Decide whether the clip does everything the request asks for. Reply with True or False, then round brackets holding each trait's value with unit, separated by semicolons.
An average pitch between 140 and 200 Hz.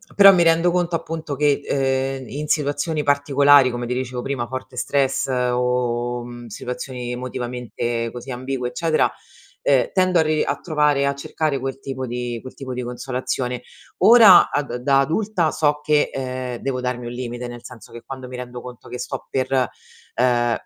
False (130 Hz)